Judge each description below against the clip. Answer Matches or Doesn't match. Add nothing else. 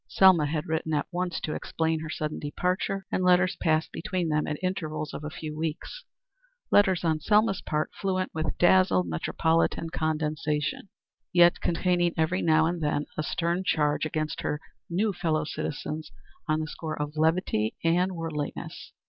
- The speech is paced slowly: Doesn't match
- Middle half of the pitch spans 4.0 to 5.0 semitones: Doesn't match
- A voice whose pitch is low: Doesn't match